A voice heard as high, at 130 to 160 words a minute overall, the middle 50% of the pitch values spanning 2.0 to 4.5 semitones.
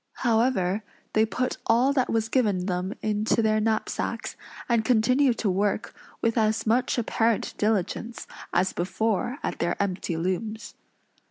Yes: high, 220 Hz; average, 140 wpm; average, 2.8 semitones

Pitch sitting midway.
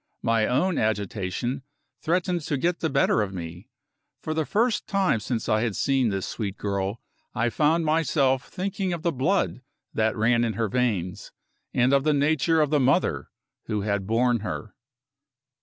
No: low, 125 Hz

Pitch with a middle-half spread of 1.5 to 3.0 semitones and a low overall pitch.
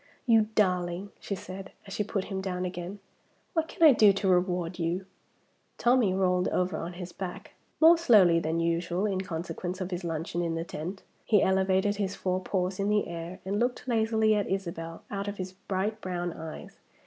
No: narrow, 2.6 semitones; medium, 185 Hz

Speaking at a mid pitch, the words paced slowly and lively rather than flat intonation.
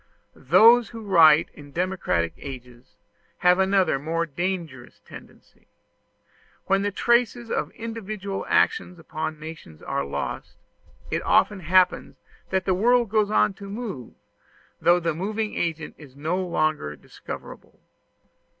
No: medium, 180 Hz; slow, 125 wpm; average, 4.7 semitones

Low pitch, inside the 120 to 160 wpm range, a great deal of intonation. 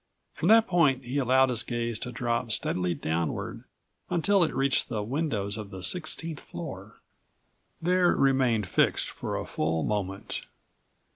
Yes: low, 125 Hz; average, 150 wpm; wide, 6.8 semitones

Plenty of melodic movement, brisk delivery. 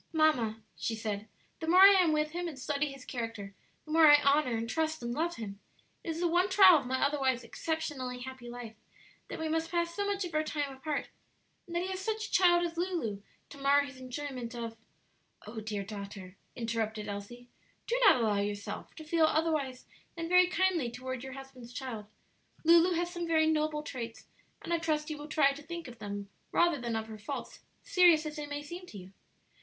Yes: wide, 5.8 semitones; fast, 215 wpm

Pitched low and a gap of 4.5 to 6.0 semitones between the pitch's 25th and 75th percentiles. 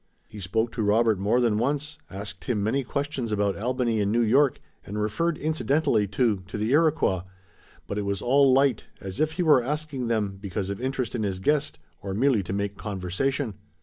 Yes: low, 115 Hz; average, 5.2 semitones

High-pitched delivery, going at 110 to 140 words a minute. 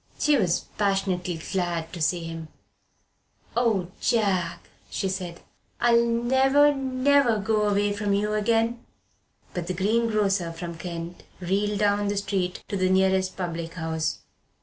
Yes: high, 195 Hz; slow, 135 wpm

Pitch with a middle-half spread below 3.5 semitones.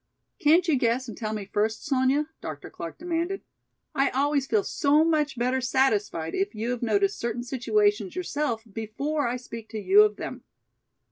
No: wide, 5.5 semitones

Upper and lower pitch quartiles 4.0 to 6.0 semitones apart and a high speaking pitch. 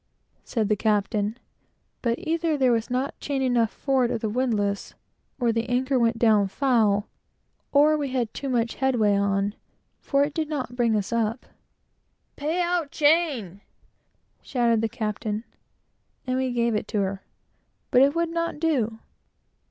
Yes: average, 4.3 semitones; high, 240 Hz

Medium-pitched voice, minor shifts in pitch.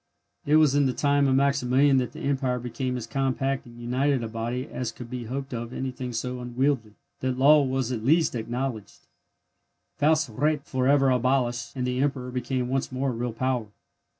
No: low, 130 Hz; narrow, 2.0 semitones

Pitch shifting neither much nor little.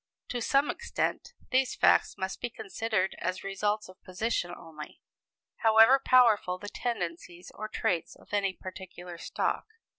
Yes: average, 4.0 semitones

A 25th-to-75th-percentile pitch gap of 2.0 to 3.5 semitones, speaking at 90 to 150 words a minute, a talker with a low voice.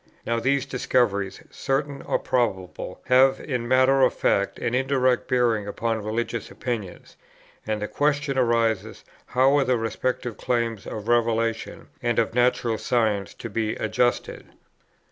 Yes: narrow, 2.5 semitones; average, 140 wpm; low, 120 Hz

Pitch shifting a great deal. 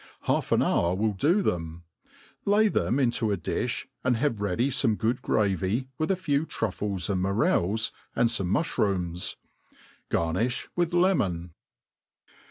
Yes: wide, 6.6 semitones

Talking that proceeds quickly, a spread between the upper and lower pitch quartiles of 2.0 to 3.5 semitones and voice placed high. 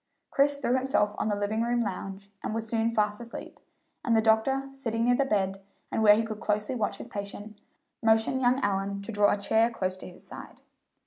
Yes: fast, 210 wpm; narrow, 2.6 semitones; high, 220 Hz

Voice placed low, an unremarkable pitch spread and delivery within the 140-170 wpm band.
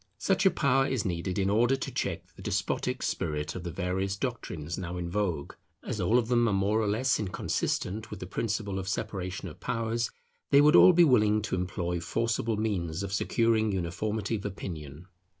No: low, 100 Hz; average, 4.1 semitones; average, 190 wpm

